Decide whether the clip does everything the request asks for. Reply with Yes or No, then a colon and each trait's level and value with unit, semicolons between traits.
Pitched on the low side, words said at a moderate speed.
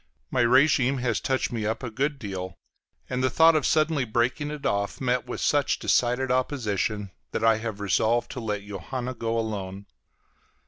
Yes: low, 120 Hz; average, 175 wpm